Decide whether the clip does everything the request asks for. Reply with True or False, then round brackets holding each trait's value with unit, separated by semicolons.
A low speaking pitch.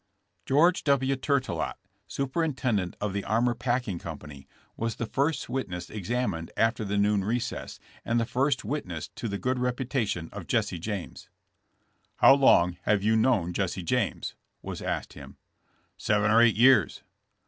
True (115 Hz)